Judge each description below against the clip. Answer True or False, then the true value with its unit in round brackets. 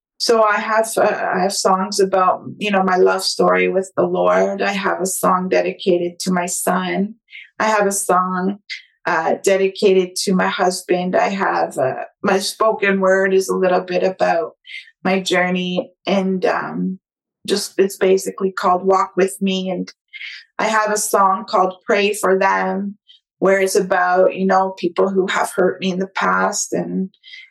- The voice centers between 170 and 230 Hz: True (190 Hz)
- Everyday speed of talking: True (170 wpm)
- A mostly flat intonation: True (1.5 semitones)